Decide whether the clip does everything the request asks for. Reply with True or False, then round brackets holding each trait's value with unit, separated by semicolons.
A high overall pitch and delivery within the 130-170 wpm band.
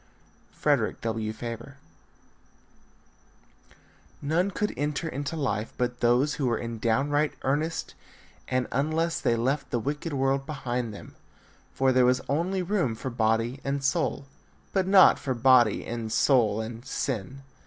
False (130 Hz; 140 wpm)